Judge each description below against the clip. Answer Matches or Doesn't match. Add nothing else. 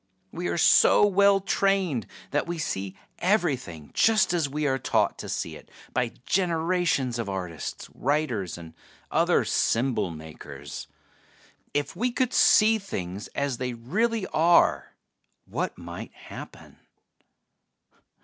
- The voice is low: Doesn't match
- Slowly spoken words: Matches